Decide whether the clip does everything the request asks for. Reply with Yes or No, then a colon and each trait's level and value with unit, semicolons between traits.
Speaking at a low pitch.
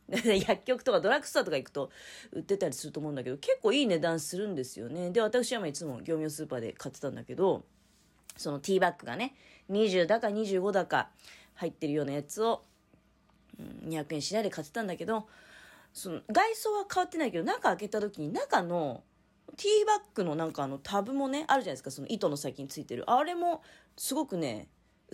No: high, 195 Hz